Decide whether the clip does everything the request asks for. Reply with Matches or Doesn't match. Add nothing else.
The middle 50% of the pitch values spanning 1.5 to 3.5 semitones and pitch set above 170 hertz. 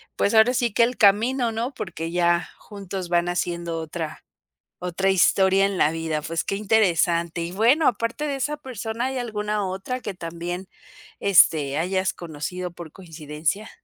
Doesn't match